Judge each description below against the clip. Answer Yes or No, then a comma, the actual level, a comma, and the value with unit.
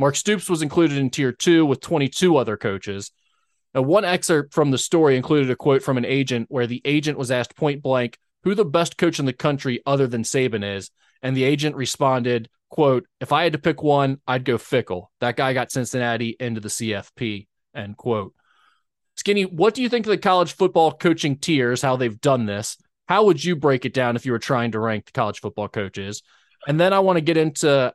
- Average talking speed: No, fast, 220 wpm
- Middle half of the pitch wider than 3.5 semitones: Yes, average, 4.7 semitones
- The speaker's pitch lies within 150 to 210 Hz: No, low, 135 Hz